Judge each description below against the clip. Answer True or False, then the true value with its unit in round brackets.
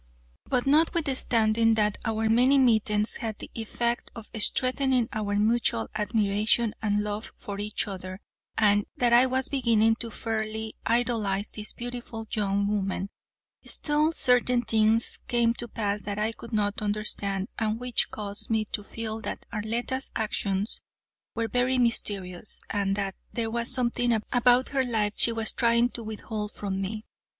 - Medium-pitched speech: False (220 Hz)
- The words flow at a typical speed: True (150 wpm)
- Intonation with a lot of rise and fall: False (2.5 semitones)